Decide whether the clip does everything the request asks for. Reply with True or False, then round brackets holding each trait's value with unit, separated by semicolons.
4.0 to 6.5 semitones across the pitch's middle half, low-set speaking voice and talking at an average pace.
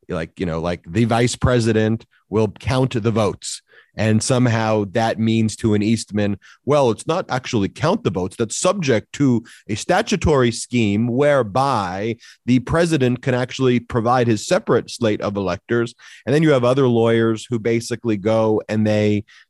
False (2.4 semitones; 115 Hz; 165 wpm)